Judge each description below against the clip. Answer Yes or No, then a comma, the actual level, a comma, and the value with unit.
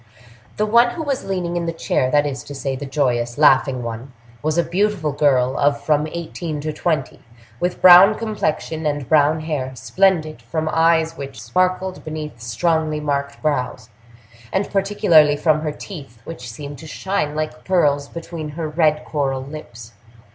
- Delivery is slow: No, average, 160 wpm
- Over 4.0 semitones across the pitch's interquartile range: No, average, 3.6 semitones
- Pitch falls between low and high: Yes, medium, 155 Hz